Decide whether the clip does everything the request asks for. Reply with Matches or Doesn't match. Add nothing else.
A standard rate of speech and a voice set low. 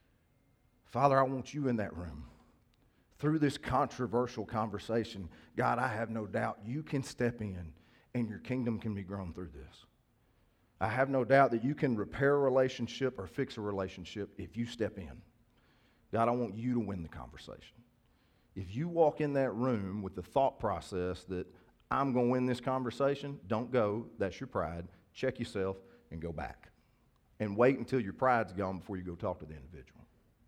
Matches